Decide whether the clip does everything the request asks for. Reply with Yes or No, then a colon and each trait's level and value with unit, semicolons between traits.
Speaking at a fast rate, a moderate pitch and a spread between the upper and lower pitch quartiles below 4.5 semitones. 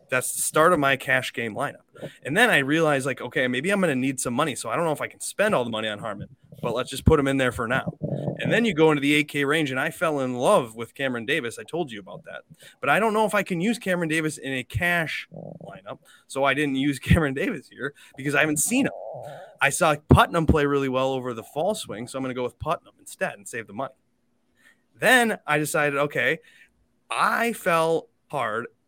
Yes: fast, 245 wpm; medium, 145 Hz; average, 3.8 semitones